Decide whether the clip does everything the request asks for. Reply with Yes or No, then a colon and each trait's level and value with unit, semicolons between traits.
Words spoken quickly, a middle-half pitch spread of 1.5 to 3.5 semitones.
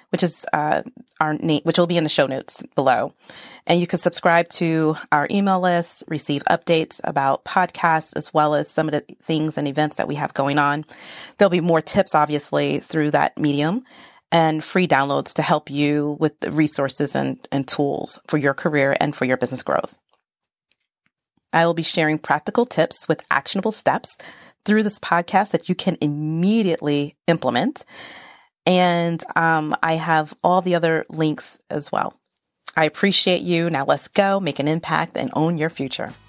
No: average, 175 wpm; average, 3.1 semitones